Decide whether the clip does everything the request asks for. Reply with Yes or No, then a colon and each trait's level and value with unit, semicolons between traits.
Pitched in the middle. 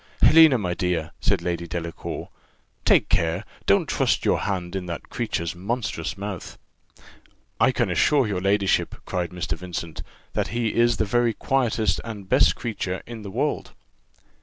No: very low, 95 Hz